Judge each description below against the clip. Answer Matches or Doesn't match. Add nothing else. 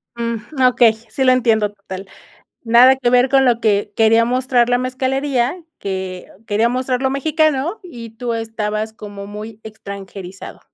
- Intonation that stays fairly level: Doesn't match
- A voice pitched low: Doesn't match